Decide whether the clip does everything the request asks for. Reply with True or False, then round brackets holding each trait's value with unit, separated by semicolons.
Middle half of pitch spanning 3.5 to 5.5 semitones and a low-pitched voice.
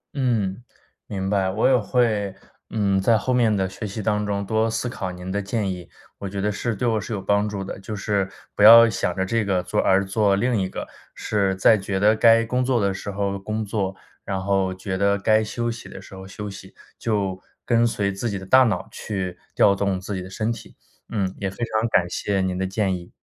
False (2.4 semitones; 100 Hz)